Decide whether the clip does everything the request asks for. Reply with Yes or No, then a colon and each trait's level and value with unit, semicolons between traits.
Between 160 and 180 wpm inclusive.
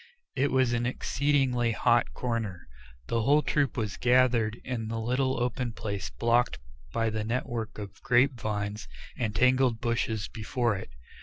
No: average, 150 wpm